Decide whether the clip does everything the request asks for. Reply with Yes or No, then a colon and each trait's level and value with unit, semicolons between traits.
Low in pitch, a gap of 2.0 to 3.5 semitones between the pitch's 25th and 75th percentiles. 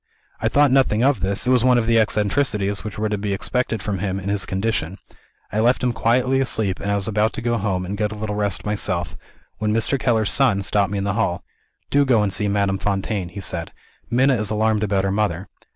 Yes: low, 105 Hz; narrow, 2.6 semitones